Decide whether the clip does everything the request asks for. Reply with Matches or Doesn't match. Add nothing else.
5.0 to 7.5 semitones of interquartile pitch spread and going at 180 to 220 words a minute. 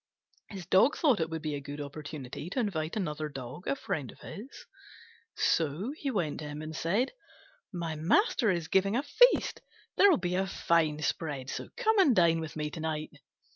Matches